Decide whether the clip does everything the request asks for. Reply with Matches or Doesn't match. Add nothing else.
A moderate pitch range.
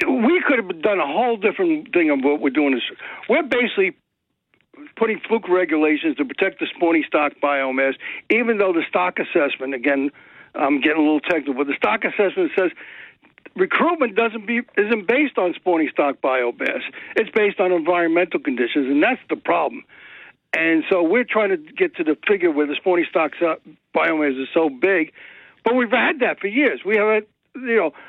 Doesn't match